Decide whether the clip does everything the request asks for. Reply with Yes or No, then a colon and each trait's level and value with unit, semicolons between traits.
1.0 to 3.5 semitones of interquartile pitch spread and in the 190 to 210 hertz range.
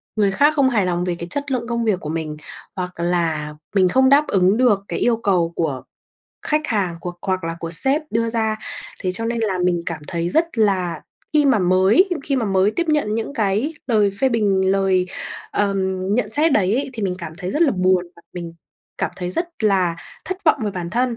No: average, 5.1 semitones; high, 200 Hz